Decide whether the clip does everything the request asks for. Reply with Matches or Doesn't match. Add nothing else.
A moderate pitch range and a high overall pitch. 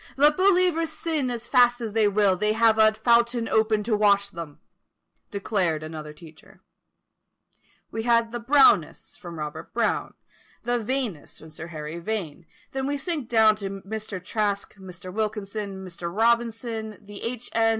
Matches